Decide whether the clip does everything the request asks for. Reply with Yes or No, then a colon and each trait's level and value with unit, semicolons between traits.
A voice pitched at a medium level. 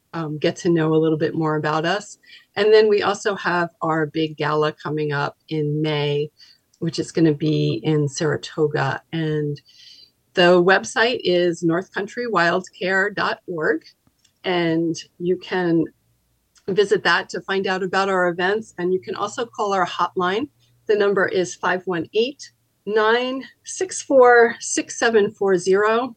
Yes: medium, 180 Hz